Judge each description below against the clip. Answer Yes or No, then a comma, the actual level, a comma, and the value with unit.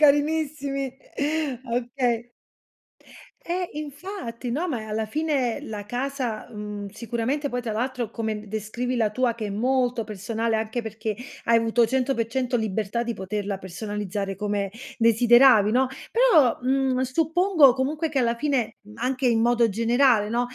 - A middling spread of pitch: Yes, average, 3.5 semitones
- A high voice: Yes, high, 240 Hz